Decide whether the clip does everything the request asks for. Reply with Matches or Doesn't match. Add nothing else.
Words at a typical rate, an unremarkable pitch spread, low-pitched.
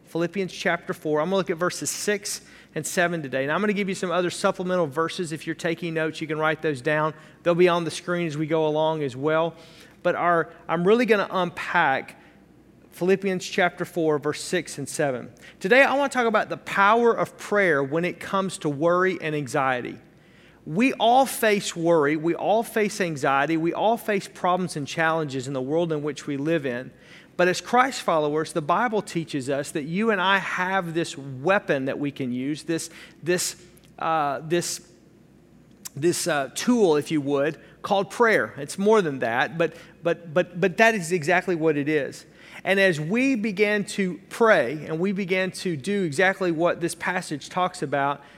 Doesn't match